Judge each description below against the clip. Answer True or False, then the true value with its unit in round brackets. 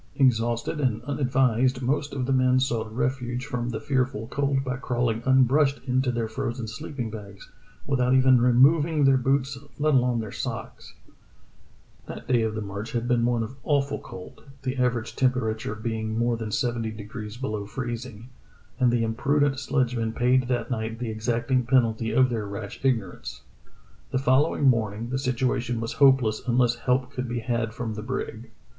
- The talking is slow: False (170 wpm)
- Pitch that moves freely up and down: False (2.5 semitones)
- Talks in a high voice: False (125 Hz)